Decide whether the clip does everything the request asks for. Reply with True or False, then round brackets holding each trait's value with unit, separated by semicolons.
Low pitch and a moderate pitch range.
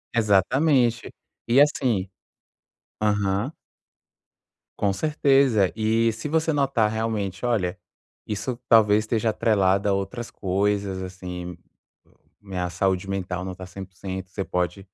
True (100 Hz; 3.6 semitones)